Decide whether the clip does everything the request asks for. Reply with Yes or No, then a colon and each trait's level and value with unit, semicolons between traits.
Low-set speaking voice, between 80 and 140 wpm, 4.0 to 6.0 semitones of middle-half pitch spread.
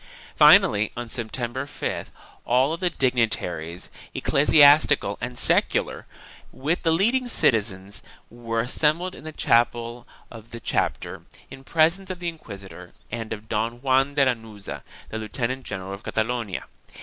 Yes: low, 120 Hz; slow, 135 wpm; average, 4.7 semitones